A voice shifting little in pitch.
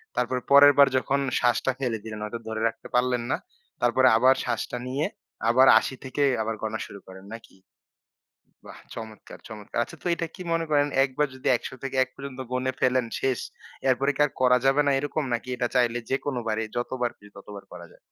No: average, 3.1 semitones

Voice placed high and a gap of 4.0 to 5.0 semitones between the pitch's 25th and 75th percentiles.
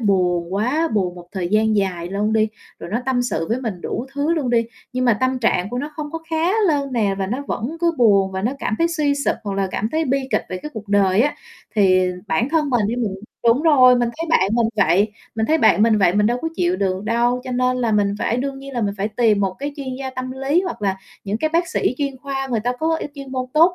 No: high, 235 Hz; wide, 5.5 semitones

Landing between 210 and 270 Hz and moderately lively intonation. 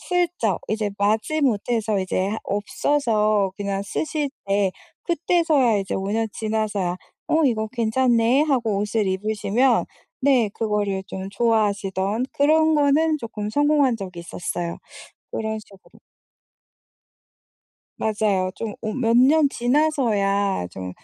Yes: high, 220 Hz; average, 4.9 semitones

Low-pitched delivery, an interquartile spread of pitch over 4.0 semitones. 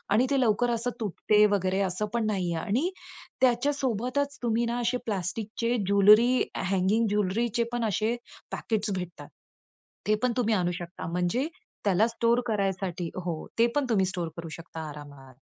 No: high, 215 Hz; average, 4.5 semitones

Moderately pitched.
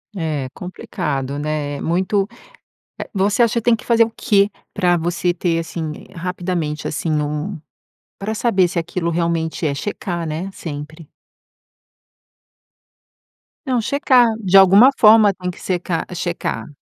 Yes: medium, 175 Hz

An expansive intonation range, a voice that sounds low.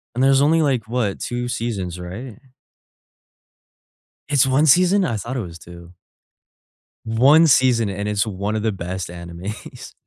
Yes: wide, 5.8 semitones; low, 115 Hz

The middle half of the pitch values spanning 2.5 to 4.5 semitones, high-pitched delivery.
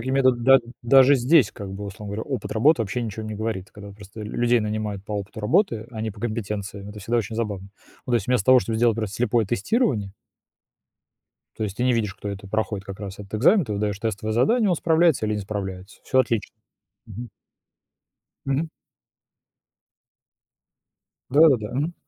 No: average, 3.4 semitones; low, 110 Hz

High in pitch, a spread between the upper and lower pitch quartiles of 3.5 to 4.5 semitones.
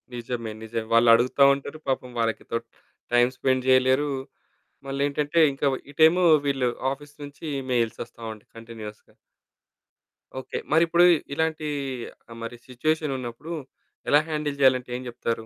No: low, 130 Hz; average, 3.9 semitones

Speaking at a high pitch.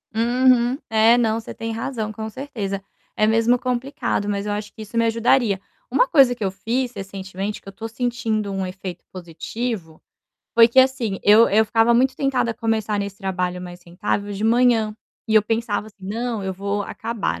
Yes: high, 220 Hz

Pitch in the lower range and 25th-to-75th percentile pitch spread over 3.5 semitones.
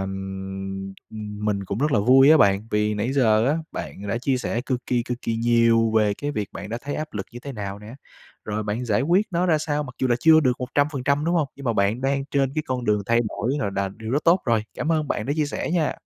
Yes: low, 120 Hz; average, 5.3 semitones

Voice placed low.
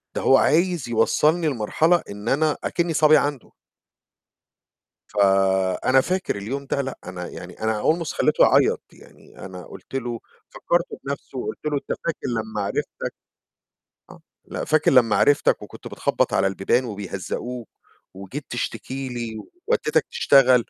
Yes: low, 125 Hz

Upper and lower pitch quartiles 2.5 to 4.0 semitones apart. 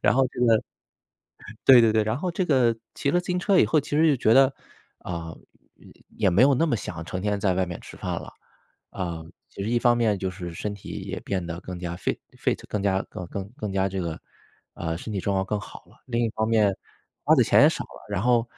No: average, 4.6 semitones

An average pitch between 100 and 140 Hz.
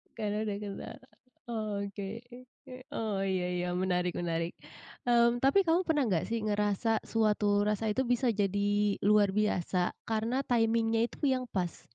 No: high, 210 Hz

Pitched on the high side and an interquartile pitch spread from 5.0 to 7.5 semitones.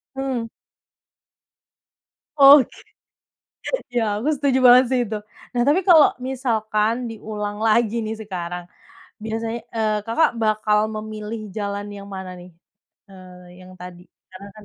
No: high, 215 Hz; average, 3.1 semitones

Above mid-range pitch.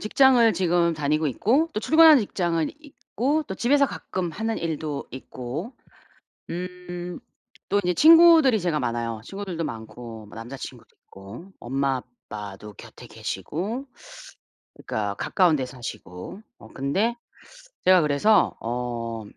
No: medium, 170 Hz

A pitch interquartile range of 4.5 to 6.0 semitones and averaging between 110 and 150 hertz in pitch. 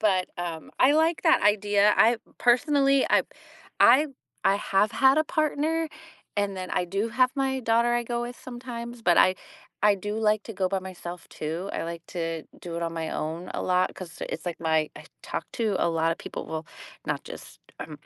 No: wide, 5.6 semitones; high, 205 Hz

